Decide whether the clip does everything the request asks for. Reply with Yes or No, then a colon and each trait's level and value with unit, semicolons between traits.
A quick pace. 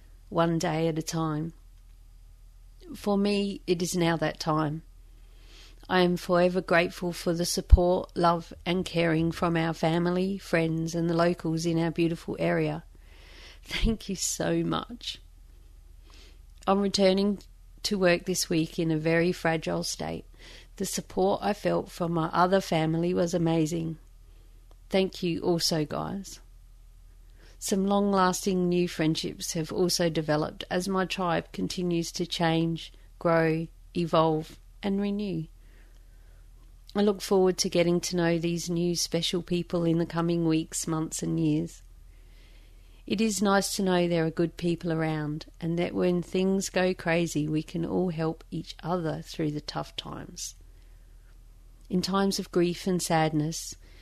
No: average, 145 wpm